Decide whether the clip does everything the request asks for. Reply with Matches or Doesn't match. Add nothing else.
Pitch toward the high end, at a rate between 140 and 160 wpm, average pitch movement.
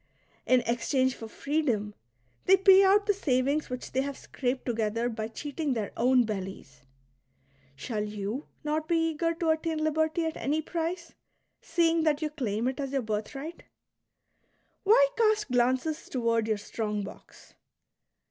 Doesn't match